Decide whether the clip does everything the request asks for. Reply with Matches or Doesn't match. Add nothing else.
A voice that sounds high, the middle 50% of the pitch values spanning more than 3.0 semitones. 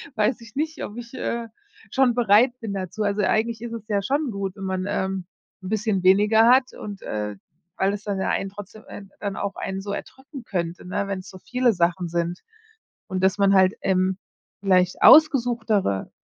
Matches